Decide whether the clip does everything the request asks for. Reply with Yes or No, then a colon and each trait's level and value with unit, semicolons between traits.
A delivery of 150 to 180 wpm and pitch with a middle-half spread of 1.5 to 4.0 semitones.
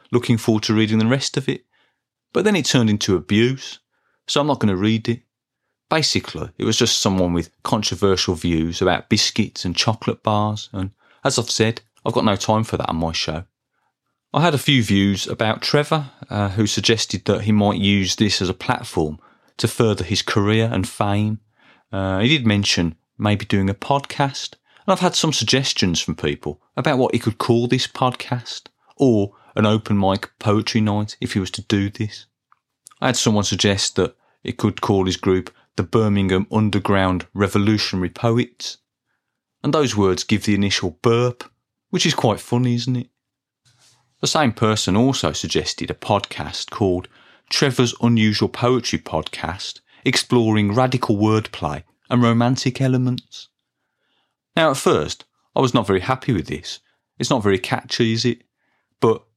Yes: average, 170 wpm; average, 3.7 semitones